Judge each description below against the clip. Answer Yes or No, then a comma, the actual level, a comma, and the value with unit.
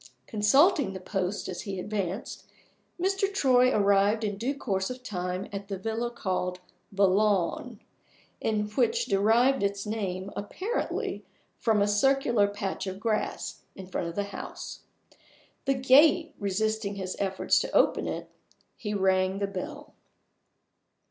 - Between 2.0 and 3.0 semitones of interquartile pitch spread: No, average, 3.8 semitones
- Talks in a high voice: Yes, high, 205 Hz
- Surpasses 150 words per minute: No, slow, 135 wpm